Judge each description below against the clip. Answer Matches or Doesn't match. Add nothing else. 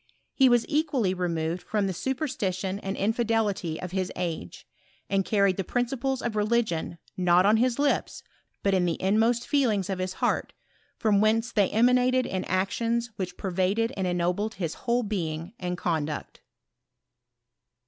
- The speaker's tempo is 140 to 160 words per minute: Matches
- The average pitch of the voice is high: Matches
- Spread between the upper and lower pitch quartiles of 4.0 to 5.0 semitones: Matches